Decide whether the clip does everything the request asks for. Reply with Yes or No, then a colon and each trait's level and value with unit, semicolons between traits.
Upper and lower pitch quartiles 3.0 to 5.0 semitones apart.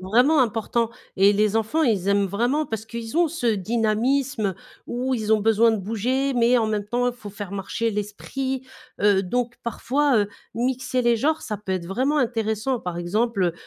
Yes: average, 3.5 semitones